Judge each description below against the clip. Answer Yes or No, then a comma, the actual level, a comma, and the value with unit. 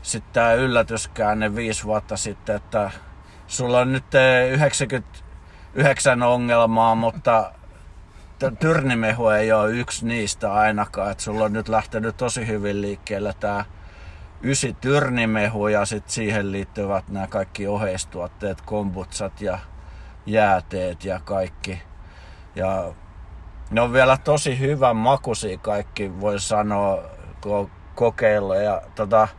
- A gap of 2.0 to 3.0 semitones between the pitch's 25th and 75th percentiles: No, average, 3.6 semitones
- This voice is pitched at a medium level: No, low, 105 Hz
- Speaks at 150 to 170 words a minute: No, average, 110 wpm